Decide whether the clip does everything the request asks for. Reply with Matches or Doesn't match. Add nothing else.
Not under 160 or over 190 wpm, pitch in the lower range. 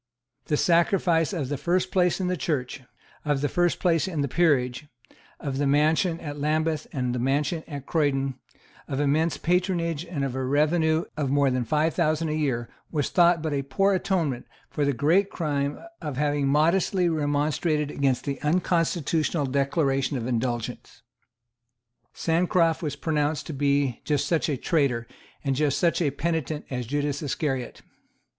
Doesn't match